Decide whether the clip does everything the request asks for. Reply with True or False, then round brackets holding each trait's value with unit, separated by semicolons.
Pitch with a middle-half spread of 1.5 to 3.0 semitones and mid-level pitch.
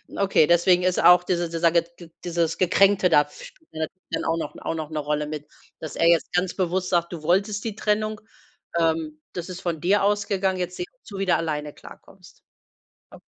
True (2.7 semitones; 175 Hz)